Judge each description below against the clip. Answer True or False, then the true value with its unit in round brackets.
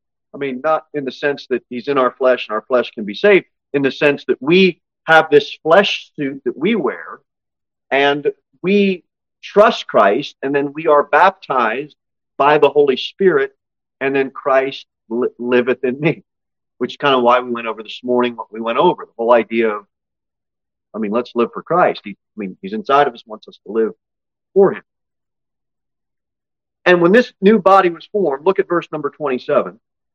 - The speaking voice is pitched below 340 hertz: True (140 Hz)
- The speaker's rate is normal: True (195 wpm)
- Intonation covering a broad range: True (6.5 semitones)